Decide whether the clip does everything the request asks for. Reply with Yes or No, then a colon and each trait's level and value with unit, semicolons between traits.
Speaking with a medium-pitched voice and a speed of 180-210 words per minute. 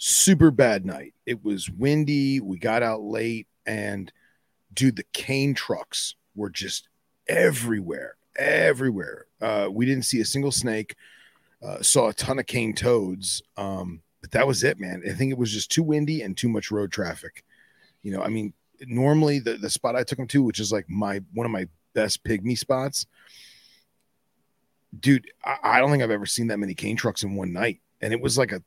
No: low, 110 Hz; average, 195 wpm